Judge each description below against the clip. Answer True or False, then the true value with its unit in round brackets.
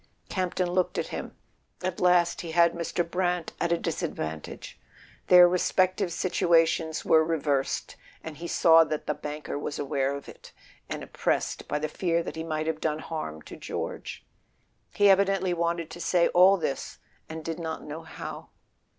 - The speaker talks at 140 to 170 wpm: True (165 wpm)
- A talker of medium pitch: True (165 Hz)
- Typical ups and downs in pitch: False (2.3 semitones)